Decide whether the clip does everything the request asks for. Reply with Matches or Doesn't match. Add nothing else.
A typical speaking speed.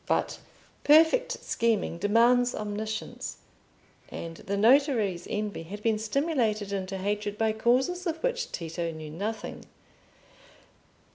Doesn't match